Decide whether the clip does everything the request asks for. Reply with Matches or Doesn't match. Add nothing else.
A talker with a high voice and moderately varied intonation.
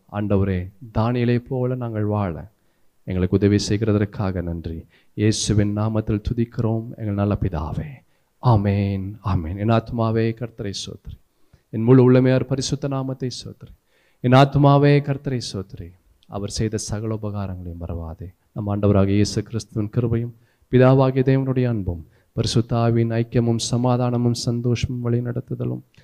Doesn't match